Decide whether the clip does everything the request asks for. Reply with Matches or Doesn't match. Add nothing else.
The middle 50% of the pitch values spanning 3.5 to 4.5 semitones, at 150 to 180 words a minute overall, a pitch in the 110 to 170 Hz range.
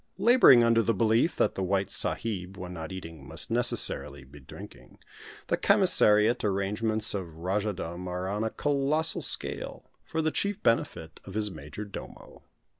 Doesn't match